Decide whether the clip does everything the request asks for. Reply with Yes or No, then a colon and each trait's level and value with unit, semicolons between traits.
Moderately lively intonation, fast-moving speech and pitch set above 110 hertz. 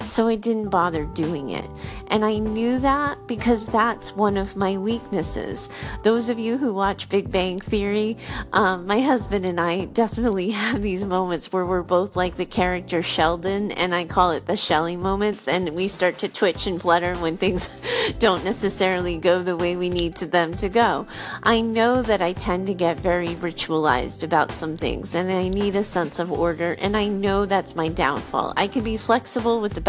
No: average, 3.4 semitones; average, 195 wpm; high, 190 Hz